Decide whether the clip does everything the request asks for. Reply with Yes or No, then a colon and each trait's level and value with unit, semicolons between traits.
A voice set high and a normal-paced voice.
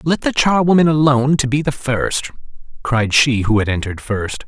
No: low, 135 Hz; average, 190 wpm